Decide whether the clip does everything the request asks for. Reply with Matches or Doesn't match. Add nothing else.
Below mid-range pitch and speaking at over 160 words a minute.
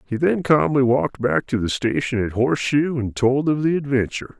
Matches